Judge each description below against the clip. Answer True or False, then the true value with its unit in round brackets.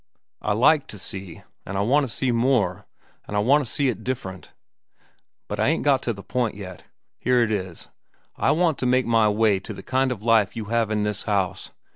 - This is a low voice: True (115 Hz)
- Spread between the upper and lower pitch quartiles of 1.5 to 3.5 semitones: False (4.1 semitones)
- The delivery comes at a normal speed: False (220 wpm)